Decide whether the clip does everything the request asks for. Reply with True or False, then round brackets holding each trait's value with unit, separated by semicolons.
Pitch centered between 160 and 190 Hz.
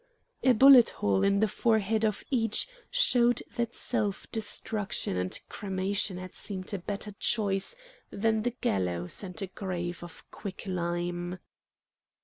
False (200 Hz)